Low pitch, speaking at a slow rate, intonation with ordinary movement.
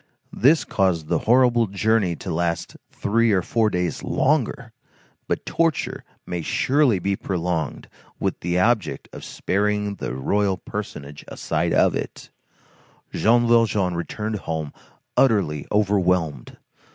Yes: low, 100 Hz; slow, 125 wpm; average, 4.6 semitones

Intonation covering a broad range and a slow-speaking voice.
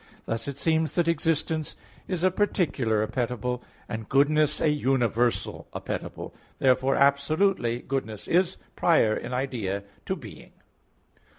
No: average, 5.0 semitones; slow, 120 wpm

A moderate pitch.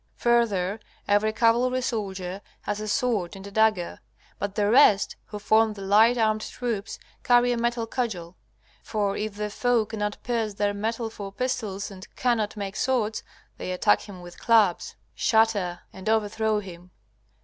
No: high, 215 Hz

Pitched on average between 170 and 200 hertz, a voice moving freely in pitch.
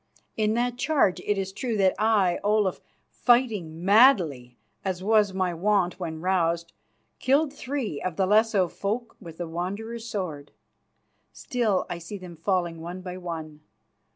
No: high, 190 Hz; average, 4.2 semitones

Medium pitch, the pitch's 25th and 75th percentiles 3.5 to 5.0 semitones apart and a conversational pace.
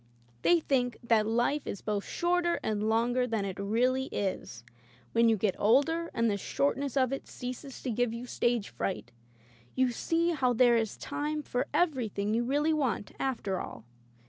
No: high, 245 Hz; average, 4.0 semitones; average, 175 wpm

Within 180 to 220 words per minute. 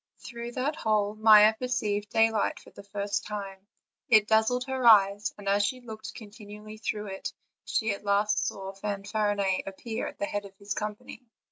No: average, 170 wpm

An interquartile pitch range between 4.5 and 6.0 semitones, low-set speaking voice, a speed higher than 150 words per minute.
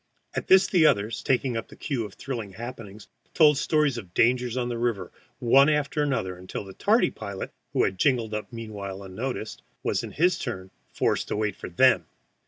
Yes: average, 5.1 semitones; low, 115 Hz; average, 190 wpm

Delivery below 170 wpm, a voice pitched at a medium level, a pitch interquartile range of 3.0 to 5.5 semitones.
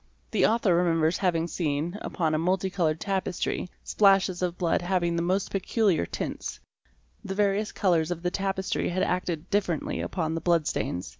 No: average, 160 wpm; medium, 180 Hz; narrow, 2.5 semitones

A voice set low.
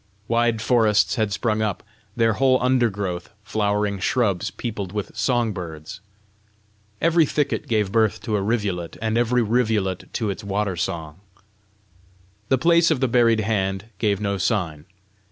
Yes: low, 105 Hz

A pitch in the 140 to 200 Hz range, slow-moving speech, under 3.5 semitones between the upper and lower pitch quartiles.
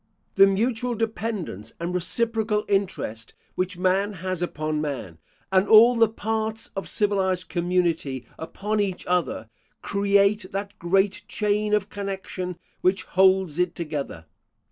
Yes: high, 190 Hz; slow, 125 wpm; average, 3.0 semitones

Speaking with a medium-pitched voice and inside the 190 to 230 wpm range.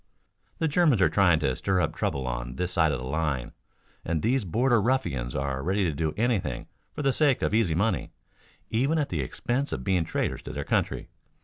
No: very low, 90 Hz; fast, 205 wpm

